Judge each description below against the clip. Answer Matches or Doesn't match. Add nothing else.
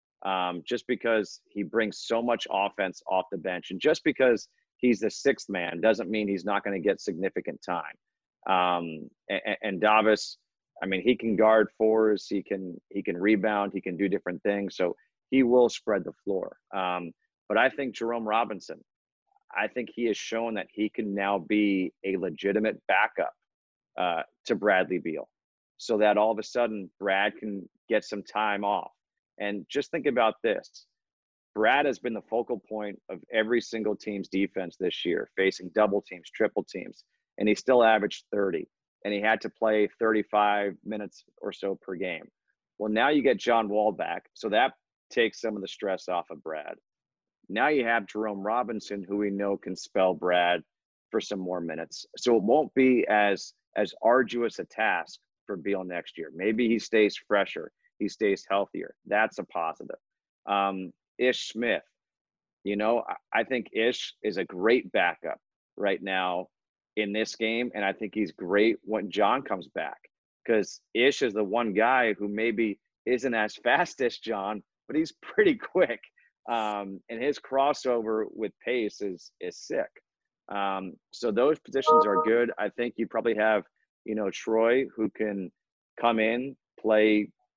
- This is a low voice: Matches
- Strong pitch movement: Doesn't match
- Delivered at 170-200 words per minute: Matches